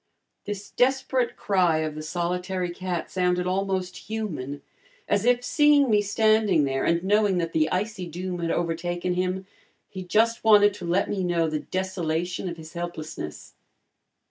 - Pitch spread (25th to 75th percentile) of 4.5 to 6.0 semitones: No, average, 3.4 semitones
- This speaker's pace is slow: No, average, 155 wpm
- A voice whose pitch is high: No, medium, 180 Hz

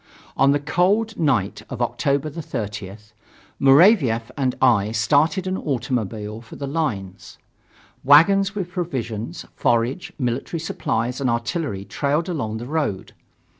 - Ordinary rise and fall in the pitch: No, wide, 6.2 semitones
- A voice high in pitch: No, low, 135 Hz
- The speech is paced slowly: Yes, slow, 125 wpm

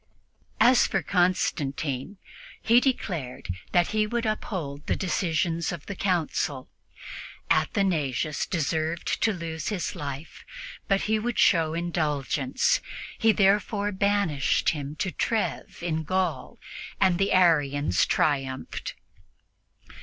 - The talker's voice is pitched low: No, medium, 170 Hz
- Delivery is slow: Yes, slow, 110 wpm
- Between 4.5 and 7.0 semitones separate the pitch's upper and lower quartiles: Yes, average, 5.1 semitones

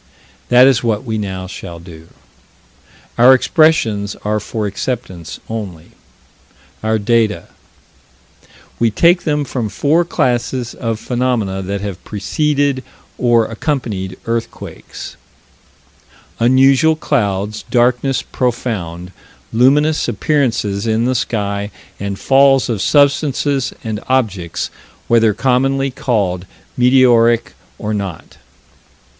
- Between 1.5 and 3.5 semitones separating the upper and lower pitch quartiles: No, average, 4.5 semitones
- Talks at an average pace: No, slow, 105 wpm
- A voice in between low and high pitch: No, low, 115 Hz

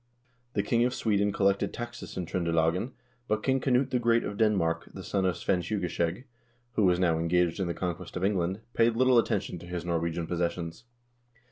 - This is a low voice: Yes, very low, 95 Hz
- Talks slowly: No, average, 200 wpm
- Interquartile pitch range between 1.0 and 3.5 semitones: No, average, 4.8 semitones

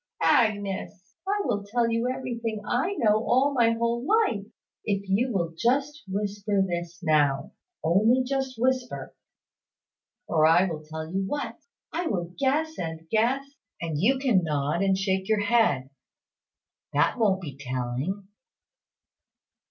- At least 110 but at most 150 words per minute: Yes, slow, 135 wpm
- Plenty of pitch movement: Yes, wide, 6.4 semitones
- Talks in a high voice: Yes, high, 205 Hz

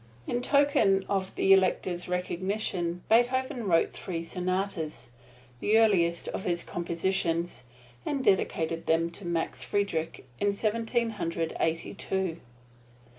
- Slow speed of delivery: Yes, slow, 120 wpm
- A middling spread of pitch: Yes, average, 3.5 semitones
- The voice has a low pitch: No, medium, 185 Hz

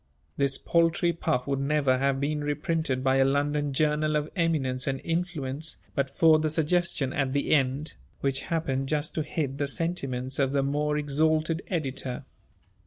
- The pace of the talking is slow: No, average, 165 wpm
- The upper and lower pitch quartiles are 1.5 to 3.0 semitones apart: Yes, average, 2.7 semitones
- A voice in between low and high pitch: Yes, medium, 145 Hz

